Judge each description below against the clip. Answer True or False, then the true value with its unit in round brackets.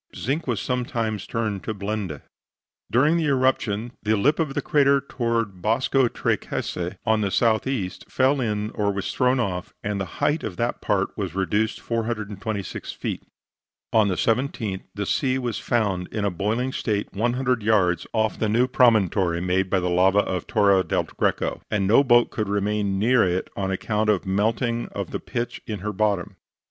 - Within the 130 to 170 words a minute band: False (180 wpm)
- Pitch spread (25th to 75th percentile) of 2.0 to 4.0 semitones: True (3.5 semitones)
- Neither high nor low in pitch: False (110 Hz)